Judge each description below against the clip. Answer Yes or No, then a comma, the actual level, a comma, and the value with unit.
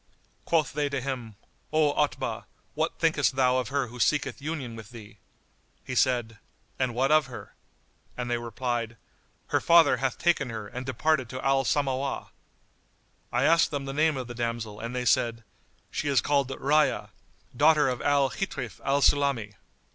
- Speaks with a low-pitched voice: Yes, low, 130 Hz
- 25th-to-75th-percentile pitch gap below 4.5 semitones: Yes, average, 3.1 semitones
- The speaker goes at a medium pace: Yes, average, 170 wpm